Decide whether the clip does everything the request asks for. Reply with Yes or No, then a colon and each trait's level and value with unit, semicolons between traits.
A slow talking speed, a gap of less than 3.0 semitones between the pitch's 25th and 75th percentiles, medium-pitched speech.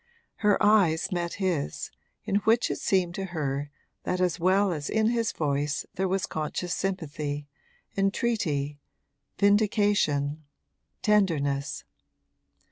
No: slow, 115 wpm; wide, 5.4 semitones; medium, 180 Hz